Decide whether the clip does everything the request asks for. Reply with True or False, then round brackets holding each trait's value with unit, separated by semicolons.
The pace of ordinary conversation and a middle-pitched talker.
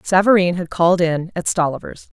True (165 wpm; 175 Hz)